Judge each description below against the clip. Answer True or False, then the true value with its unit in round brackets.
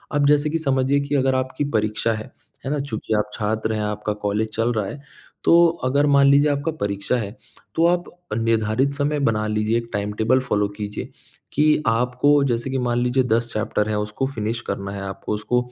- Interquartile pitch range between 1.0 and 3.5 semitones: False (4.7 semitones)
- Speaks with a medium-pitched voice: False (120 Hz)